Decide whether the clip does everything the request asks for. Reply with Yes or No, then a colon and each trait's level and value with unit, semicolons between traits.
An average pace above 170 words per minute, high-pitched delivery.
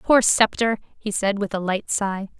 Yes: average, 200 wpm; high, 205 Hz